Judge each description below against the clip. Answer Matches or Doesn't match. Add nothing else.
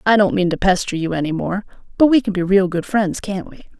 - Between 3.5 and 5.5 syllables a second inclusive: Doesn't match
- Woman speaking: Matches